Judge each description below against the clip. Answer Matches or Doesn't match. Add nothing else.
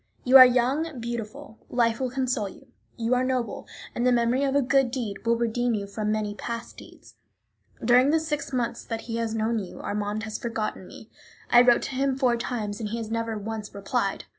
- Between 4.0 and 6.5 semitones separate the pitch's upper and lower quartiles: Doesn't match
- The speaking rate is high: Matches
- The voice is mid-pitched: Doesn't match